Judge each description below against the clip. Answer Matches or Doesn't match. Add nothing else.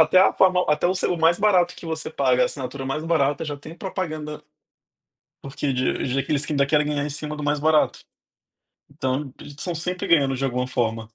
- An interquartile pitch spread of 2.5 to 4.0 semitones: Matches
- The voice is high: Doesn't match